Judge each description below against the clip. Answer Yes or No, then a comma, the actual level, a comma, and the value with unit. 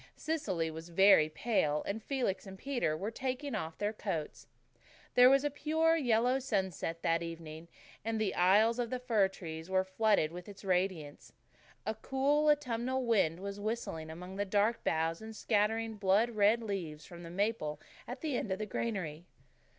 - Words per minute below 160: No, average, 175 wpm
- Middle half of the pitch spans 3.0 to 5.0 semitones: No, wide, 5.6 semitones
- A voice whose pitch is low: No, high, 205 Hz